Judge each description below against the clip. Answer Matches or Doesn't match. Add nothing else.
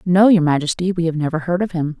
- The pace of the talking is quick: Matches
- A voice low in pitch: Doesn't match